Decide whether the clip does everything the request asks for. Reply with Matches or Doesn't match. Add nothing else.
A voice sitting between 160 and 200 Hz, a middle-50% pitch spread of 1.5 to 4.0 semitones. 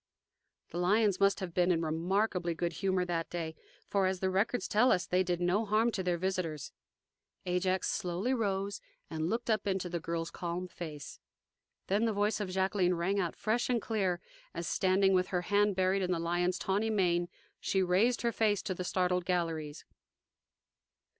Matches